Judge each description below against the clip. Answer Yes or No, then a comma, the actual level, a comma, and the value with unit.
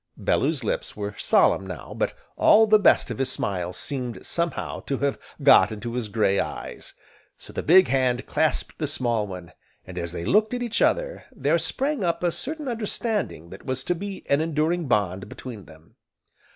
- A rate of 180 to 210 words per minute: Yes, average, 185 wpm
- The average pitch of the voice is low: Yes, low, 130 Hz